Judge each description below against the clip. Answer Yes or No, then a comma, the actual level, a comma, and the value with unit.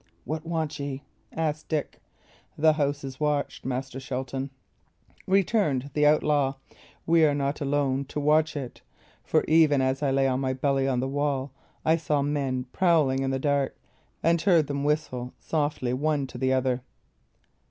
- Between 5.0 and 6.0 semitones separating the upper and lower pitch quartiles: No, narrow, 2.4 semitones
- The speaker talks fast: No, average, 165 wpm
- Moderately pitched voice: Yes, medium, 145 Hz